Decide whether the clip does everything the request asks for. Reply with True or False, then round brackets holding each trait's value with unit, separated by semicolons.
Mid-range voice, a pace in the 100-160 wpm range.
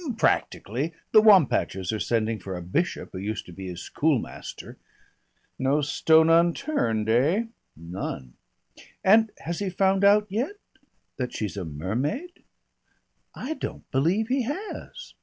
True (150 Hz; 140 wpm)